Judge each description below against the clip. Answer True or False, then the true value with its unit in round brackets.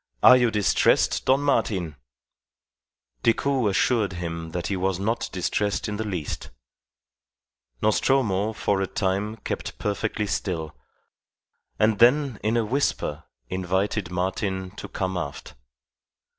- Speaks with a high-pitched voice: False (100 Hz)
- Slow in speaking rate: True (120 wpm)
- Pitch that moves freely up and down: False (3.2 semitones)